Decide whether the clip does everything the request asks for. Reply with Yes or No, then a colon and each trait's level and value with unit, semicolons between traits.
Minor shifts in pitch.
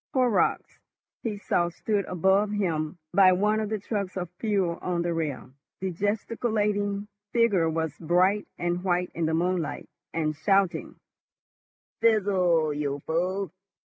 No: average, 3.5 semitones